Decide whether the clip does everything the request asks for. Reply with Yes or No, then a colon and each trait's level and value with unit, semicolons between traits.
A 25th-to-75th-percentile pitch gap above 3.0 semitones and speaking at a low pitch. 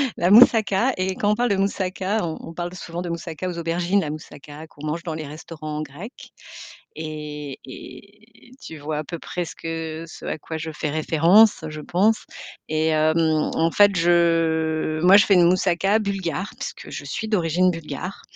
No: average, 3.5 semitones; medium, 170 Hz